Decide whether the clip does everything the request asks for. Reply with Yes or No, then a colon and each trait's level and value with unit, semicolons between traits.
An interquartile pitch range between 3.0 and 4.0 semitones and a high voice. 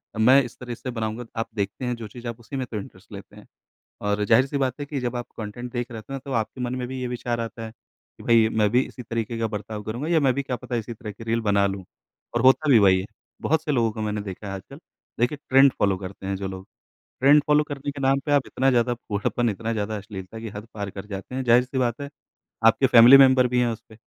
No: average, 3.5 semitones; low, 120 Hz